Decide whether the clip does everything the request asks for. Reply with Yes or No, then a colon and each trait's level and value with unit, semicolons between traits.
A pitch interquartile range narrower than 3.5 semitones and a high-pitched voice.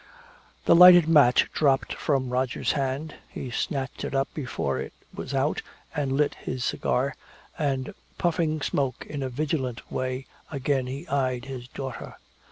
No: narrow, 2.4 semitones; low, 135 Hz